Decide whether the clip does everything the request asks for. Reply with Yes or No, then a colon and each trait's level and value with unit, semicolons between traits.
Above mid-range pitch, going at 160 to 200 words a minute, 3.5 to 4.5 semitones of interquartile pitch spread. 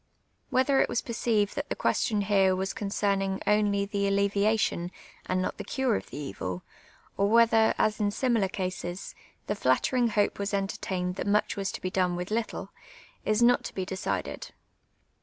No: high, 200 Hz; average, 190 wpm; narrow, 2.4 semitones